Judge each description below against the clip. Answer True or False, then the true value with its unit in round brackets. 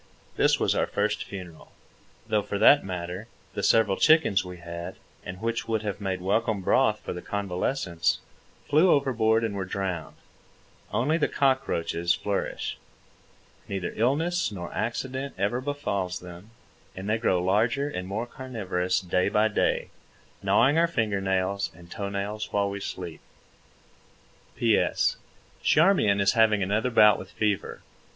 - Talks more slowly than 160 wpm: True (145 wpm)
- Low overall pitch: True (100 Hz)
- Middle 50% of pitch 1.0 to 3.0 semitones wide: False (3.8 semitones)